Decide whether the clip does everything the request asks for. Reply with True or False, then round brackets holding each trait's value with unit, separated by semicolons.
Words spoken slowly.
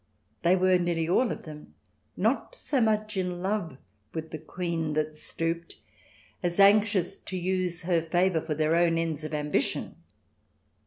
False (155 wpm)